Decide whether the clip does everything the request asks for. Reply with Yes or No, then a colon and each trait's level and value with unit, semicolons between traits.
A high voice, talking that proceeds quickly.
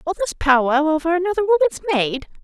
No: very high, 330 Hz; average, 175 wpm